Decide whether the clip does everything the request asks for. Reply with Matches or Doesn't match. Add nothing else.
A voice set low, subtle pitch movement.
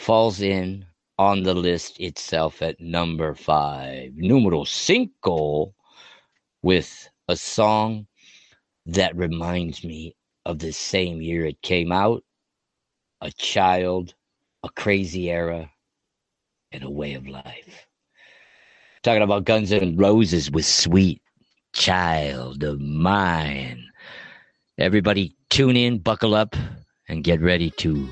Doesn't match